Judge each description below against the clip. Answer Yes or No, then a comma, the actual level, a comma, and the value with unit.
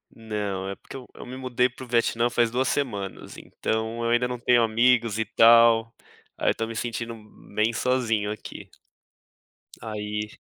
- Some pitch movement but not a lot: No, narrow, 1.9 semitones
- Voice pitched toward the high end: No, low, 115 Hz